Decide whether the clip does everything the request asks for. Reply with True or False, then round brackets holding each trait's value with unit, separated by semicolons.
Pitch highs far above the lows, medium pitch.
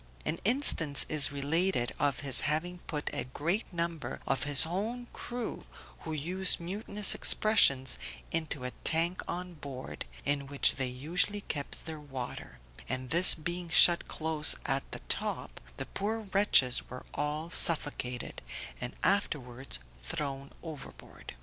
False (4.6 semitones; 155 Hz)